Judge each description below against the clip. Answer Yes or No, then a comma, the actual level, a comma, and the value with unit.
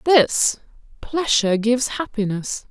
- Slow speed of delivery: Yes, slow, 65 wpm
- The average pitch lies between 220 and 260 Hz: Yes, high, 240 Hz